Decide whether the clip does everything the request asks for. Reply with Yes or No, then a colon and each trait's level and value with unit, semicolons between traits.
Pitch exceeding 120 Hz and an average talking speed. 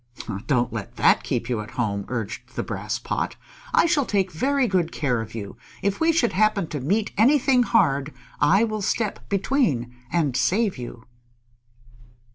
Yes: medium, 185 Hz; average, 165 wpm